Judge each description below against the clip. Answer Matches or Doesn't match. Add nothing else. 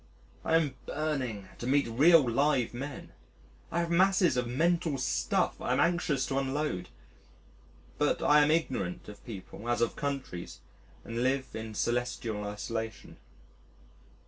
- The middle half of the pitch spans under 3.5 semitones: Doesn't match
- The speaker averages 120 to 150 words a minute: Matches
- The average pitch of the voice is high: Doesn't match